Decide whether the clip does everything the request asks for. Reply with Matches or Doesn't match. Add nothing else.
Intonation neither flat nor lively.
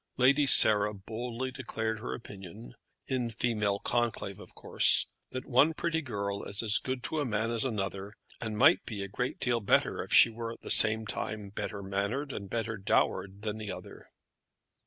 Matches